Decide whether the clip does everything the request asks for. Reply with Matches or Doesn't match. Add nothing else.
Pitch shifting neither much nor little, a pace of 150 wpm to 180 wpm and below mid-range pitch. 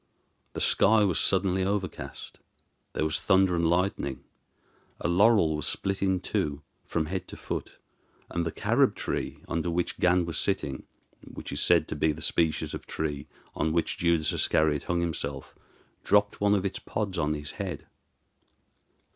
Matches